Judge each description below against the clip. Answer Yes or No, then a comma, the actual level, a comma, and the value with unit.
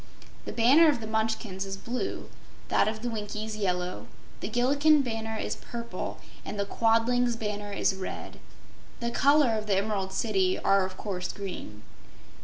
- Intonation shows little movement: No, average, 3.2 semitones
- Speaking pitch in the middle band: No, high, 220 Hz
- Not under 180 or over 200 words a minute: No, average, 160 wpm